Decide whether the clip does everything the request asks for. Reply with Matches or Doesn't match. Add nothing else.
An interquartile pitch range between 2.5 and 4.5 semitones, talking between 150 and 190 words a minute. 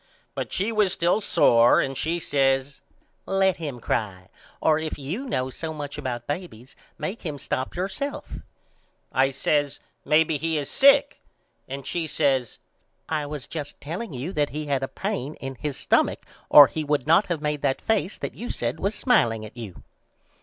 Matches